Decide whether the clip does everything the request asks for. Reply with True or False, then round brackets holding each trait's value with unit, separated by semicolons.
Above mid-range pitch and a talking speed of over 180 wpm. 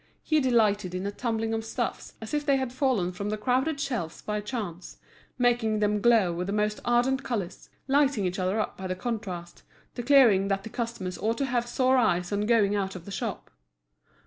True (220 Hz; 200 wpm)